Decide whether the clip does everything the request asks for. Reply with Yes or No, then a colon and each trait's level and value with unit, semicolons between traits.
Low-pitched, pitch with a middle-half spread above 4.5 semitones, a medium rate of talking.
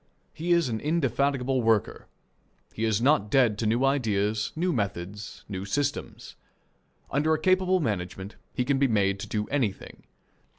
Yes: low, 120 Hz; wide, 5.6 semitones; average, 155 wpm